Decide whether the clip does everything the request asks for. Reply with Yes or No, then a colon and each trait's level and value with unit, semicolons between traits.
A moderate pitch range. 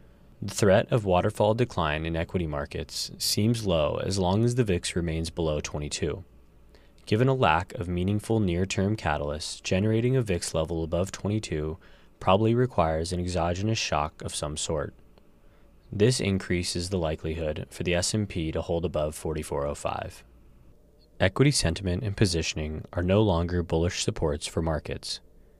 Yes: average, 4.8 semitones